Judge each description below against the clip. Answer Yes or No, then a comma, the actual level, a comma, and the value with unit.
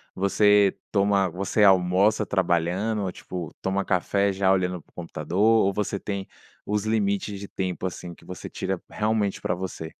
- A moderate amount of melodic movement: No, narrow, 2.0 semitones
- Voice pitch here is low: Yes, very low, 95 Hz